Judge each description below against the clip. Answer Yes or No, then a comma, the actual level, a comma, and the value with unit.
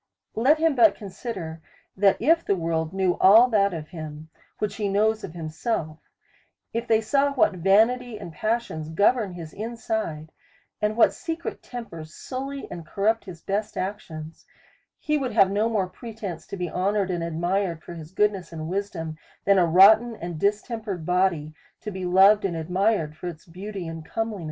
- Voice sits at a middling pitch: No, high, 195 Hz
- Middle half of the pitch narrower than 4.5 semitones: No, average, 4.8 semitones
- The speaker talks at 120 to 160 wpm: No, average, 175 wpm